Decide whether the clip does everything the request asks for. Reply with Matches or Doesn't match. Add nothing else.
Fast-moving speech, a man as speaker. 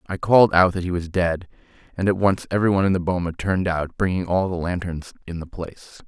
Matches